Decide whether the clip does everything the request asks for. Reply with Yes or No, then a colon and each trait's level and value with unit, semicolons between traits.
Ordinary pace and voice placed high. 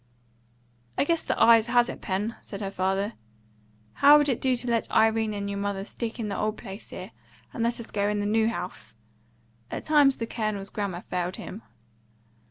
Yes: average, 190 wpm; high, 215 Hz